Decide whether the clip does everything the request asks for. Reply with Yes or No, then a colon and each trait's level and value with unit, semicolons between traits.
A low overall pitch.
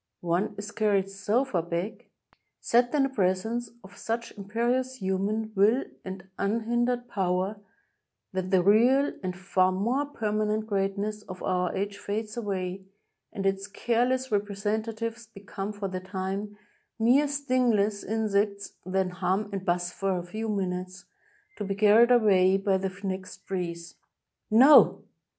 No: high, 205 Hz